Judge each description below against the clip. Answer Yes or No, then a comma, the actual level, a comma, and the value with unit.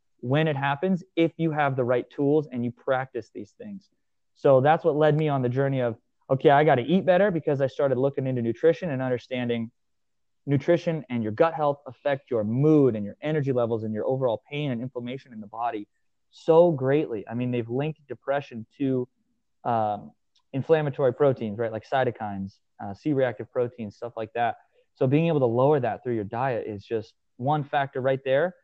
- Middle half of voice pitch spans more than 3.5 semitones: Yes, average, 4.2 semitones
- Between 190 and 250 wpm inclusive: Yes, average, 195 wpm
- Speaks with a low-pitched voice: Yes, low, 130 Hz